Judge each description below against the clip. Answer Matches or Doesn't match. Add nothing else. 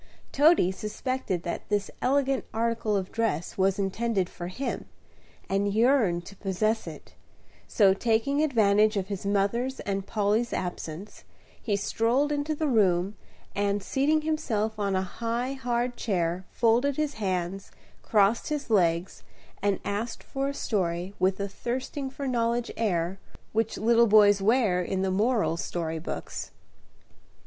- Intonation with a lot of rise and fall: Doesn't match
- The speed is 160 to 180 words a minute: Doesn't match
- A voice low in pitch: Doesn't match